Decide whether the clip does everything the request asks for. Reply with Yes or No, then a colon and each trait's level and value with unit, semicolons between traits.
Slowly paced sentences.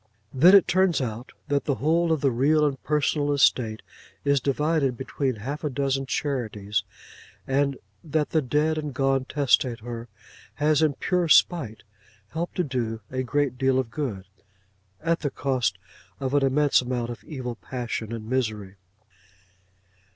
No: average, 150 wpm